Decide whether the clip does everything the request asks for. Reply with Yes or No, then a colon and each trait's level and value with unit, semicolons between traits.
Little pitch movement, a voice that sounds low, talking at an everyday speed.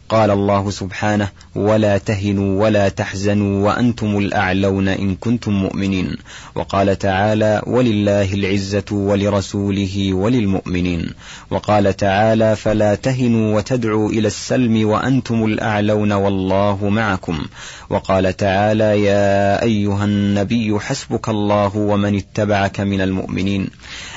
Yes: narrow, 1.5 semitones; low, 100 Hz; average, 100 wpm